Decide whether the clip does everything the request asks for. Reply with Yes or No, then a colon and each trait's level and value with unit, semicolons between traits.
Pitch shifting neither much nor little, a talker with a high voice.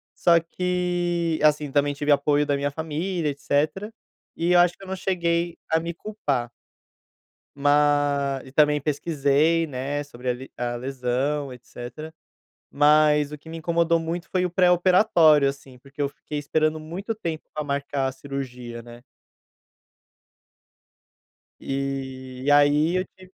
No: average, 3.3 semitones; medium, 150 Hz